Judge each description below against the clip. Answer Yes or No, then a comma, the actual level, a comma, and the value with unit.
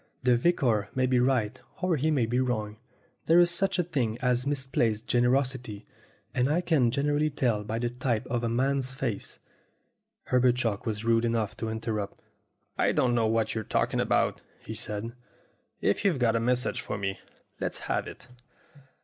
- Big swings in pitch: No, average, 3.0 semitones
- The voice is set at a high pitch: No, low, 125 Hz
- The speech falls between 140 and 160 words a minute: No, average, 185 wpm